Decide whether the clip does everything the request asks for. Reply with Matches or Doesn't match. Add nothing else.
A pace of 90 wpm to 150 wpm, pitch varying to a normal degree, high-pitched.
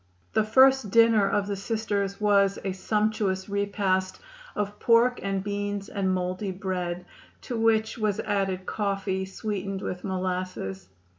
Doesn't match